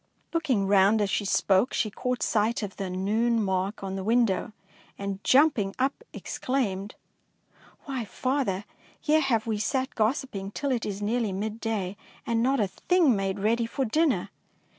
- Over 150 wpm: Yes, average, 170 wpm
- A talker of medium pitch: No, high, 220 Hz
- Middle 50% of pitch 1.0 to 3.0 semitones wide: No, average, 4.5 semitones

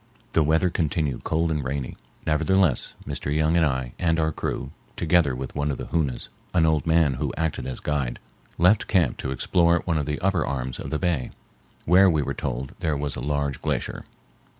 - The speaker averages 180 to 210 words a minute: Yes, average, 195 wpm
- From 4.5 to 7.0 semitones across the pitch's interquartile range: No, average, 3.3 semitones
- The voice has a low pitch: Yes, very low, 75 Hz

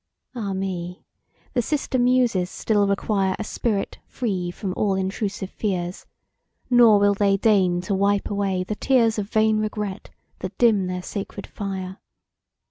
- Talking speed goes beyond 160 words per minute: No, average, 145 wpm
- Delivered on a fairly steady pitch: Yes, narrow, 2.3 semitones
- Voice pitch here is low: No, high, 200 Hz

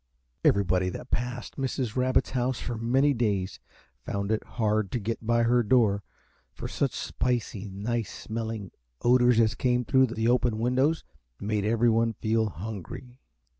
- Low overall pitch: Yes, low, 115 Hz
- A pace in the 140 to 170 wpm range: Yes, average, 145 wpm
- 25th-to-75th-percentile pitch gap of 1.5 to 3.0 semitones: Yes, narrow, 2.6 semitones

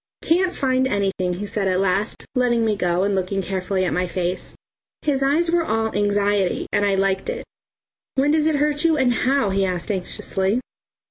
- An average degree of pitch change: No, wide, 6.1 semitones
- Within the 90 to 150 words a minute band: No, average, 190 wpm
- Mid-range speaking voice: No, high, 205 Hz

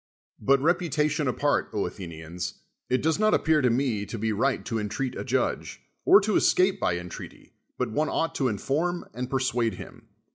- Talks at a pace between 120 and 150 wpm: No, average, 175 wpm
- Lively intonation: Yes, wide, 6.3 semitones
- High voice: No, low, 130 Hz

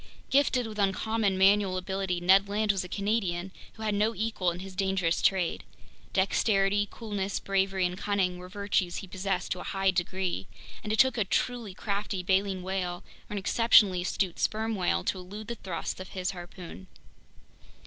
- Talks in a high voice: Yes, high, 195 Hz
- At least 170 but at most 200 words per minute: Yes, average, 175 wpm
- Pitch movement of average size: No, narrow, 2.1 semitones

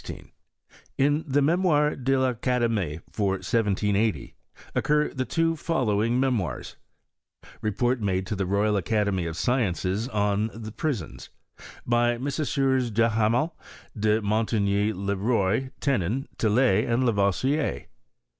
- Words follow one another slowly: Yes, slow, 115 wpm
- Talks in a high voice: No, low, 115 Hz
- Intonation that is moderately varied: Yes, average, 4.3 semitones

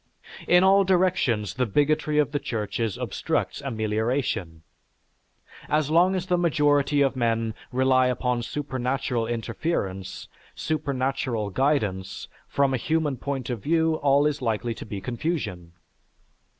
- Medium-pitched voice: No, low, 130 Hz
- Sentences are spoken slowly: Yes, slow, 125 wpm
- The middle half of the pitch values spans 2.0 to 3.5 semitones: No, average, 4.8 semitones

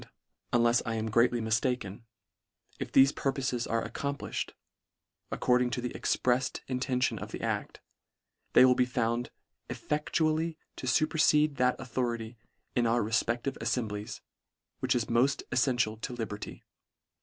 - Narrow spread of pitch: Yes, narrow, 2.2 semitones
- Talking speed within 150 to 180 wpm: No, average, 140 wpm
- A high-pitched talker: No, low, 125 Hz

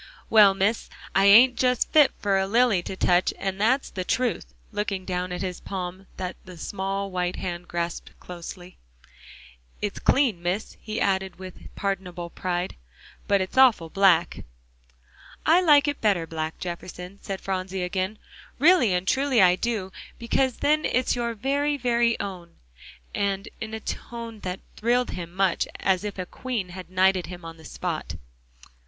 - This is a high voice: Yes, high, 195 Hz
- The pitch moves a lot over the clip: No, average, 4.3 semitones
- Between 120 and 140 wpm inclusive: No, average, 160 wpm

